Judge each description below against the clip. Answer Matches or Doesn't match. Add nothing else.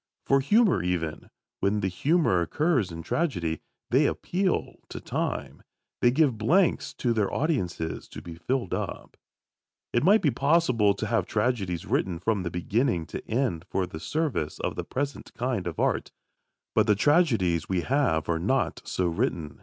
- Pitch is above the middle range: Doesn't match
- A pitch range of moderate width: Doesn't match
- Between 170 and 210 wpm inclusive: Doesn't match